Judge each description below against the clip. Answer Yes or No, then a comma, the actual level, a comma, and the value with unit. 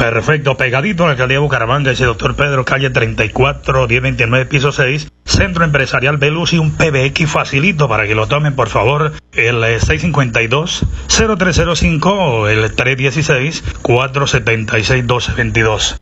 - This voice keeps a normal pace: No, slow, 115 wpm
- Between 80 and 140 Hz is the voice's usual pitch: Yes, low, 135 Hz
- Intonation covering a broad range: No, average, 4.0 semitones